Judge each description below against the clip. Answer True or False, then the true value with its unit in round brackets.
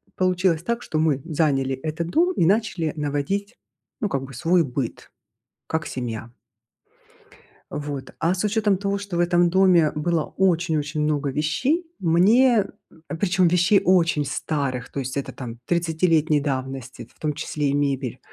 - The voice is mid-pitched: True (160 Hz)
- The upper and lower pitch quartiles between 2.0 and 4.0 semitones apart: False (4.5 semitones)